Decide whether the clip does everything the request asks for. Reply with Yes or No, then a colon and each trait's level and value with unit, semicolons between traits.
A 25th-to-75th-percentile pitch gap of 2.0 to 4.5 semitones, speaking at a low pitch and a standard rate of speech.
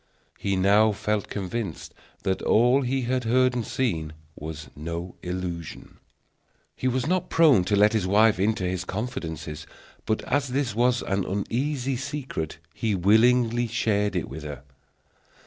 No: average, 5.2 semitones; low, 105 Hz; average, 145 wpm